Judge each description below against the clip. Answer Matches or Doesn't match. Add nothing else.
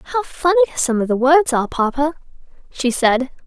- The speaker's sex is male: Doesn't match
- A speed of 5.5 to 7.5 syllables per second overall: Matches